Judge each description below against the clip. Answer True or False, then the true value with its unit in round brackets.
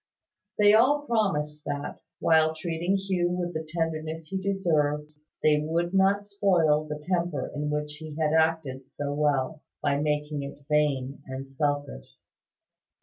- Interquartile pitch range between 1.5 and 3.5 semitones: True (2.9 semitones)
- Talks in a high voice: False (155 Hz)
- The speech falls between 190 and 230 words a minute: False (145 wpm)